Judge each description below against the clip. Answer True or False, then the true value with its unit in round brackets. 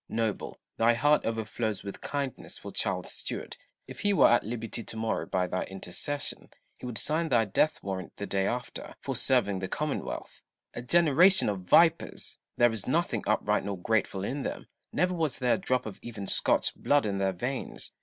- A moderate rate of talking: True (185 wpm)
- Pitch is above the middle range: False (115 Hz)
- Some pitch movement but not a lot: False (5.9 semitones)